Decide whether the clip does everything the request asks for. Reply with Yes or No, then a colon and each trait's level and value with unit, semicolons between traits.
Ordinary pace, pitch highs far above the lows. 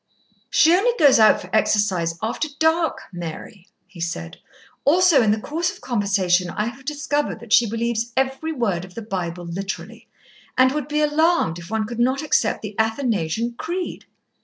Yes: average, 170 wpm; wide, 7.2 semitones